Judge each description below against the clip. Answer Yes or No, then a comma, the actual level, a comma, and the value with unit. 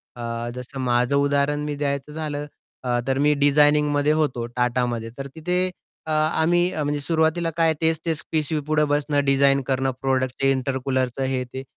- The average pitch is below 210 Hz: Yes, medium, 140 Hz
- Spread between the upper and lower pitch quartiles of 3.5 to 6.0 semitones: No, average, 2.7 semitones